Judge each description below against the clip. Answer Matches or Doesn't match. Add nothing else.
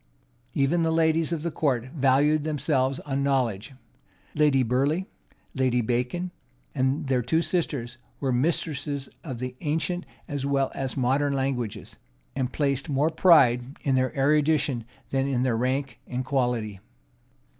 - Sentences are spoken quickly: Doesn't match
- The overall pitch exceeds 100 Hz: Matches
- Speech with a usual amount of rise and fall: Matches